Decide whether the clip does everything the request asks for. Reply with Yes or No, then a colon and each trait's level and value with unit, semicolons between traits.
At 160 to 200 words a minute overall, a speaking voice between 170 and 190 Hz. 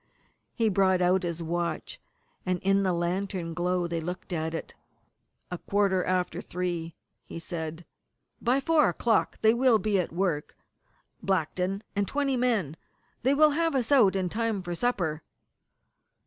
No: average, 150 wpm; medium, 185 Hz